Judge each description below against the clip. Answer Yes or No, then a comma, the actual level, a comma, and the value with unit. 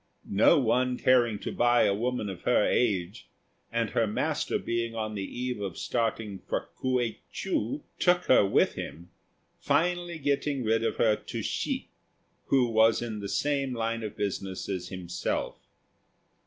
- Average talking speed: Yes, average, 155 wpm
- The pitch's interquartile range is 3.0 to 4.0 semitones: Yes, average, 3.5 semitones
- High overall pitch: No, low, 115 Hz